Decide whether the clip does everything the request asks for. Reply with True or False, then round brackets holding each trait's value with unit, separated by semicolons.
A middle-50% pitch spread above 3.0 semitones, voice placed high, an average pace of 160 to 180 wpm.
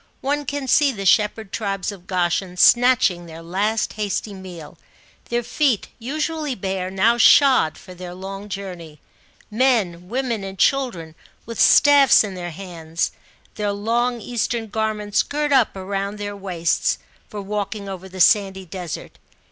False (4.4 semitones; 200 Hz; 145 wpm)